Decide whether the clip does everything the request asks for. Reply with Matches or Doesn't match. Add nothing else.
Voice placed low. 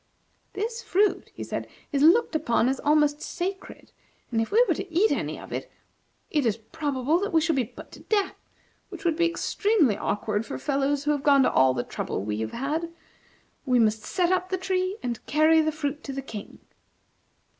Doesn't match